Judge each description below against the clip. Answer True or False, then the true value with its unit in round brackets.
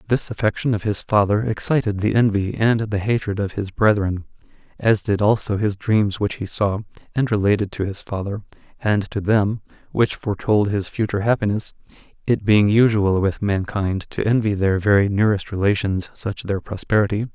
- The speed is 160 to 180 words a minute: True (170 wpm)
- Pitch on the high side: False (105 Hz)